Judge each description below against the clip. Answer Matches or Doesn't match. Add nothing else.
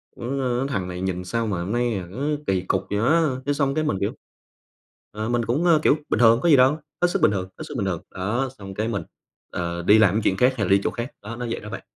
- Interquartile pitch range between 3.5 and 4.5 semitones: Doesn't match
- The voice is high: Doesn't match